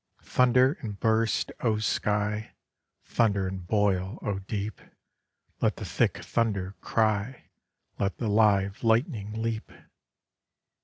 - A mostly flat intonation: Yes, narrow, 2.3 semitones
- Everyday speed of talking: No, slow, 110 wpm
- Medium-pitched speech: No, low, 105 Hz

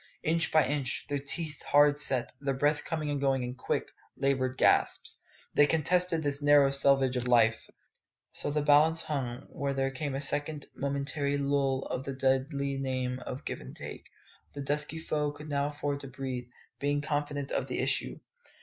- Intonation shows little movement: Yes, narrow, 1.6 semitones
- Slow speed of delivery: No, average, 175 wpm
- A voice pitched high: No, medium, 140 Hz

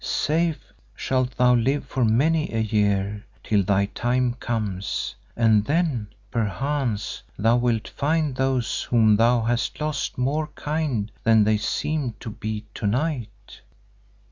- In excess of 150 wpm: No, slow, 135 wpm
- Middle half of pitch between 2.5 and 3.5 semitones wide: No, average, 4.2 semitones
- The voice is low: Yes, low, 120 Hz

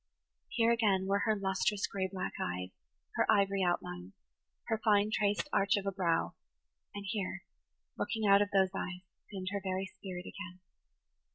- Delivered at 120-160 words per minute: Yes, average, 155 wpm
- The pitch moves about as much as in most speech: No, narrow, 1.6 semitones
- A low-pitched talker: No, high, 195 Hz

